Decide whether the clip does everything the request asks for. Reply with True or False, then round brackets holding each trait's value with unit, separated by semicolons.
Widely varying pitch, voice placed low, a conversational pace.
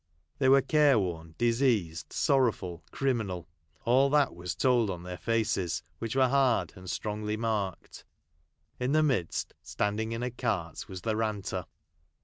True (5.8 semitones; 110 Hz; 145 wpm)